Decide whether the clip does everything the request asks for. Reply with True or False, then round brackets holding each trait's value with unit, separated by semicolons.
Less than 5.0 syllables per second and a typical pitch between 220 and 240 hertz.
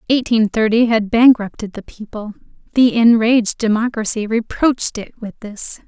True (4.8 syllables/s; 225 Hz)